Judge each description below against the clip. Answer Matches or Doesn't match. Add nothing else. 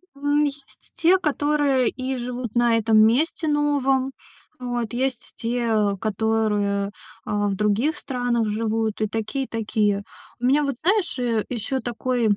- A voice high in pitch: Matches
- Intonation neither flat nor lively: Matches